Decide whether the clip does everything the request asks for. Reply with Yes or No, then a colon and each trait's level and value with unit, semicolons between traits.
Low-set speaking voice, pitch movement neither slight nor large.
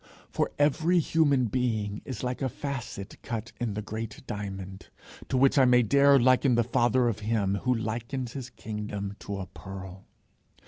Yes: low, 120 Hz; average, 3.9 semitones